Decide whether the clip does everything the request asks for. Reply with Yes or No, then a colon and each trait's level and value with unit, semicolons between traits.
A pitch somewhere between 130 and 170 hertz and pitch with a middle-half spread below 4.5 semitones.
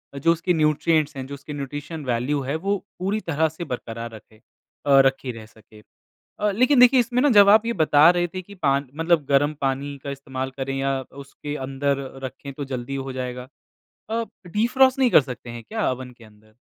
No: medium, 140 Hz; average, 4.9 semitones